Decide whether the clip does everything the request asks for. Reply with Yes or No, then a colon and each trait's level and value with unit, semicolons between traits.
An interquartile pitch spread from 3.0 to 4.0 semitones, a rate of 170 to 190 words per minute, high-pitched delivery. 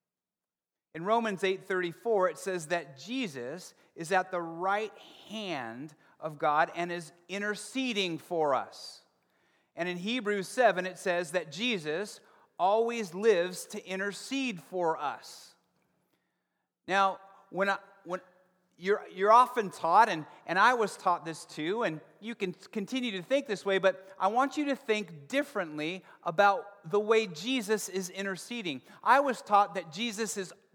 No: average, 3.3 semitones; average, 150 wpm; high, 195 Hz